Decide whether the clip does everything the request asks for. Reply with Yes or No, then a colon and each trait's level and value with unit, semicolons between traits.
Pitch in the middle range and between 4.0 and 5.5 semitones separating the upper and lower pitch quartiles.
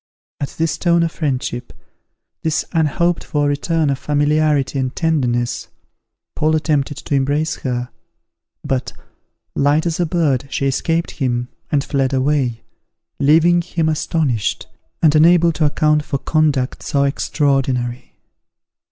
No: medium, 145 Hz; average, 2.9 semitones